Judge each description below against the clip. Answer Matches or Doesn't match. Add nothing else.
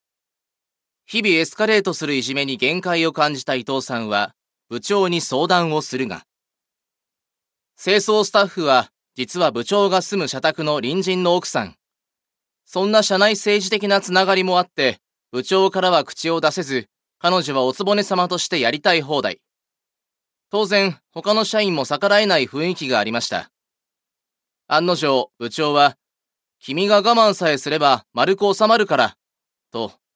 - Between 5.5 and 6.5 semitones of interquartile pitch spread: Matches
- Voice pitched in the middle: Matches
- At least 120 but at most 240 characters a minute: Doesn't match